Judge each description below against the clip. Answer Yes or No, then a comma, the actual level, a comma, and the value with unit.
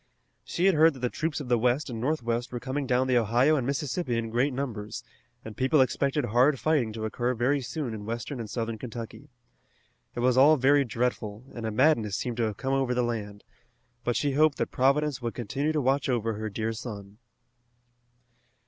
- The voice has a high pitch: No, low, 125 Hz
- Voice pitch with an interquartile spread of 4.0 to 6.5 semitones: No, average, 3.5 semitones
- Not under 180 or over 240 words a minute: Yes, average, 200 wpm